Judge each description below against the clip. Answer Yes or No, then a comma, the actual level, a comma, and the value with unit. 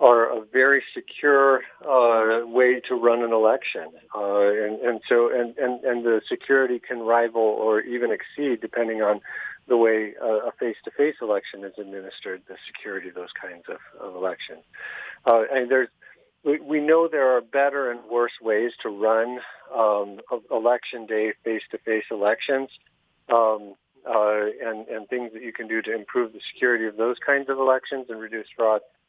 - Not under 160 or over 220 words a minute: Yes, average, 170 wpm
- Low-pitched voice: Yes, low, 115 Hz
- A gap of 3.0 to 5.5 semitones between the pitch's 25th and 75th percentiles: No, narrow, 2.5 semitones